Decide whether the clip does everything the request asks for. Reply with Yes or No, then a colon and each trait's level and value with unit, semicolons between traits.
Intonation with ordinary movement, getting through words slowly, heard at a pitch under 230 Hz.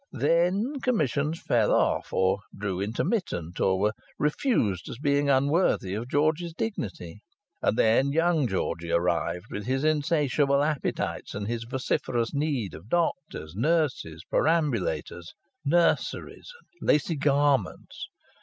No: wide, 7.6 semitones; slow, 120 wpm; medium, 140 Hz